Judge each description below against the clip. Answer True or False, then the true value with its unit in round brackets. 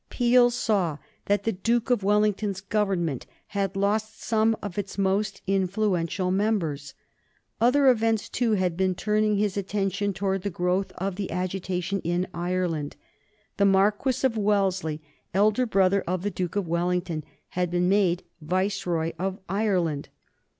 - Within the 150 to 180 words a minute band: False (140 wpm)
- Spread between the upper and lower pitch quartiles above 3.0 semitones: False (2.6 semitones)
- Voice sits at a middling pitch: False (195 Hz)